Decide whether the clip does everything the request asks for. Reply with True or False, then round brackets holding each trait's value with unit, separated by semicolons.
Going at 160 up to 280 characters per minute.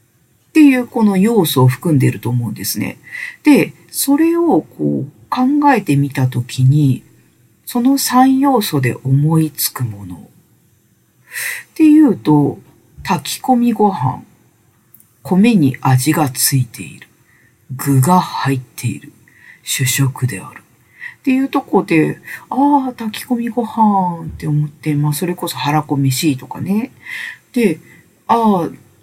True (235 characters per minute)